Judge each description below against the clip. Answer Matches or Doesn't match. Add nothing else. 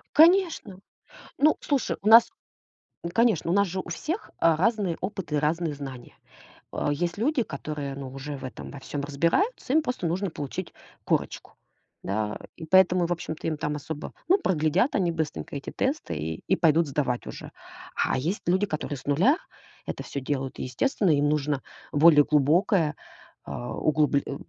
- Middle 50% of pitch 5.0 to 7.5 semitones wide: Matches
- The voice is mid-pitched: Matches